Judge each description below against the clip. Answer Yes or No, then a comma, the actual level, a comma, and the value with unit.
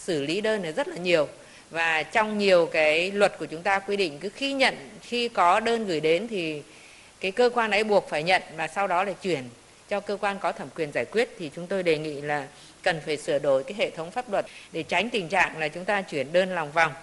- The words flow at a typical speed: No, fast, 255 wpm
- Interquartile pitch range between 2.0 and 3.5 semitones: No, average, 4.2 semitones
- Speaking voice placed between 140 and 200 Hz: Yes, medium, 185 Hz